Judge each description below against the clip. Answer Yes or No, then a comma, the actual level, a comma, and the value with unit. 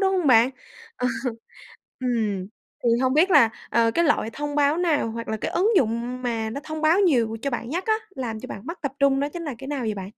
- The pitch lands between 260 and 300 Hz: Yes, very high, 265 Hz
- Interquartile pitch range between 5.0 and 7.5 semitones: Yes, average, 5.3 semitones